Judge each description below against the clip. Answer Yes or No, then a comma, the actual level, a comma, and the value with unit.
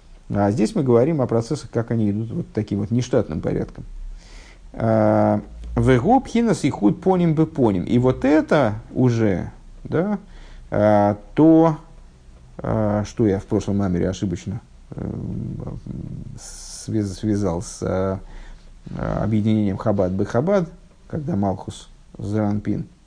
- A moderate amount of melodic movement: Yes, average, 5.0 semitones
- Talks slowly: Yes, slow, 105 wpm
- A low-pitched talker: Yes, low, 110 Hz